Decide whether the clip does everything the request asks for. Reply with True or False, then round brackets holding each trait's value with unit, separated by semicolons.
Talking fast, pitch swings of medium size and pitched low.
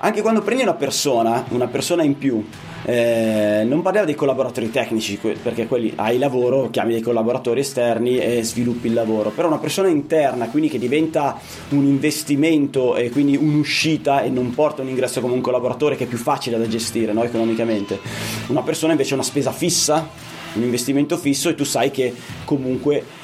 True (185 wpm; 4.1 semitones; 130 Hz)